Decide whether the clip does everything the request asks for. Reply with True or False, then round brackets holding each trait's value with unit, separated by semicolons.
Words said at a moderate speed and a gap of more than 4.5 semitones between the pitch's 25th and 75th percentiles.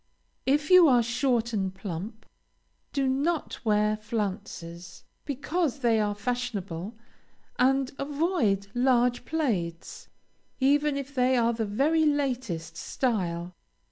False (110 wpm; 5.2 semitones)